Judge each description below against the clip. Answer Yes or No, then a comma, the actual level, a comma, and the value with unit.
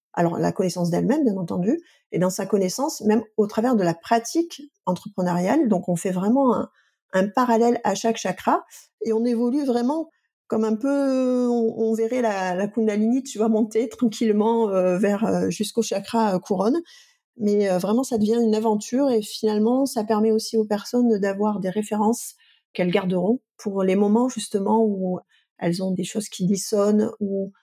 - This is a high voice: Yes, high, 220 Hz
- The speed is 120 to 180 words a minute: Yes, average, 175 wpm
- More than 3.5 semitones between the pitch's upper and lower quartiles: No, average, 3.0 semitones